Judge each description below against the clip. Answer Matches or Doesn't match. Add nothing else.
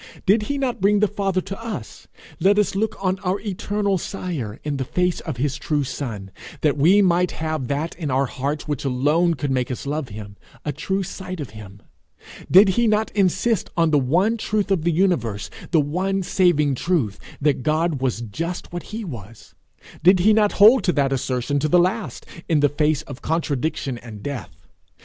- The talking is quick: Doesn't match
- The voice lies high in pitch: Doesn't match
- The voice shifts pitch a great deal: Matches